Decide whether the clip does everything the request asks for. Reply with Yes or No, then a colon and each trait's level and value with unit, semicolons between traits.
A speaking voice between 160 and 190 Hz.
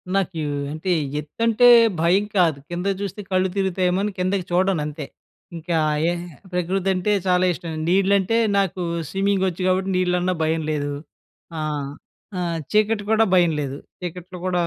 Yes: medium, 185 Hz